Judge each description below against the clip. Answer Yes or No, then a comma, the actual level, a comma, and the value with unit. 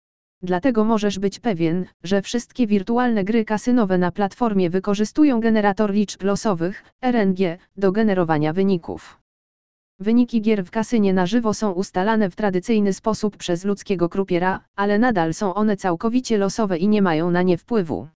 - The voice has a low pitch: No, high, 205 Hz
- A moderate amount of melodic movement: Yes, average, 3.2 semitones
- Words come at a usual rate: Yes, average, 150 wpm